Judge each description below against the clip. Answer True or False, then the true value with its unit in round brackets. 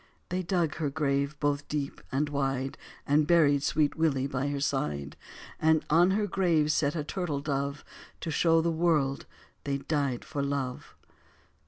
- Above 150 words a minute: True (160 wpm)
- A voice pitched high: False (145 Hz)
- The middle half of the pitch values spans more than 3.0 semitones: False (2.5 semitones)